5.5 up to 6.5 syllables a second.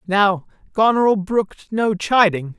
No: 4.1 syllables/s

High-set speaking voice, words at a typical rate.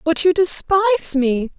Yes: very high, 330 Hz; average, 150 wpm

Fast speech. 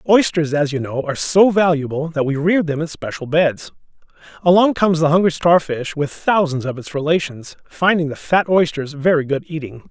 No: average, 190 wpm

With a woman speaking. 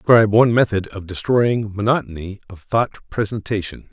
No: male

